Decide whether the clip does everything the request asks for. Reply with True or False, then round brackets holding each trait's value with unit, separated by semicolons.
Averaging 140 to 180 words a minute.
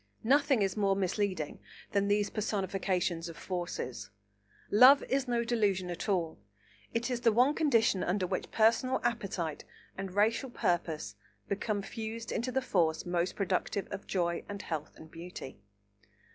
True (145 wpm)